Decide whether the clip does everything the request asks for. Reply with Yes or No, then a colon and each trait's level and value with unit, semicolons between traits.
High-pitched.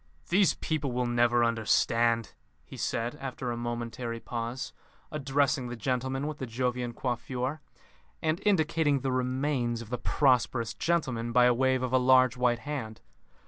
No: low, 125 Hz